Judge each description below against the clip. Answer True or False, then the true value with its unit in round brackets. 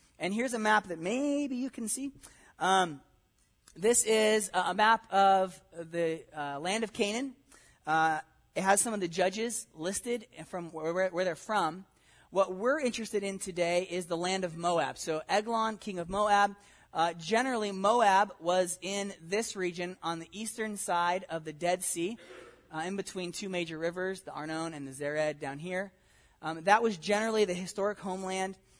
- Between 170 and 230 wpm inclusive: True (175 wpm)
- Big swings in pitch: False (3.7 semitones)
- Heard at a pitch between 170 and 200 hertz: True (190 Hz)